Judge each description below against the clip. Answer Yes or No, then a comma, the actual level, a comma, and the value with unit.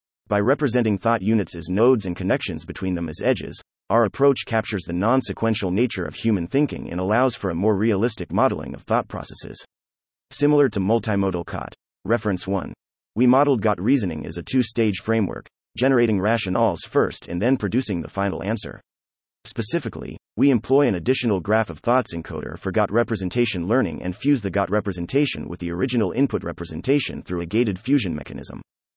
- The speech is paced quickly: No, average, 175 wpm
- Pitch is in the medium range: No, low, 105 Hz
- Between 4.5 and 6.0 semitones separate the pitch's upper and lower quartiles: Yes, wide, 5.4 semitones